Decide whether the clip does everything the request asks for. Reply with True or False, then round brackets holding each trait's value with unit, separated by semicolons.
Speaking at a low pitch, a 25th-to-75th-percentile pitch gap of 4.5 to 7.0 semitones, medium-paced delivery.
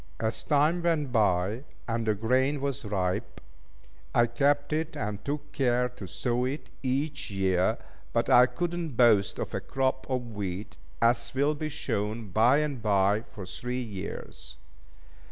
True (120 Hz; 5.0 semitones; 155 wpm)